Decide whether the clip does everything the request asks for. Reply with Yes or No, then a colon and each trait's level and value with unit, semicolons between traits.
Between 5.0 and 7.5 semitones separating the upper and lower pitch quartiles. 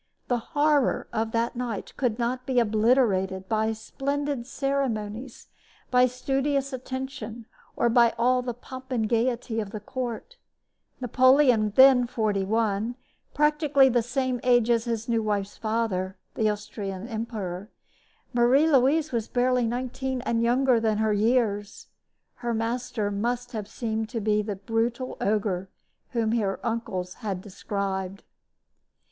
No: average, 3.0 semitones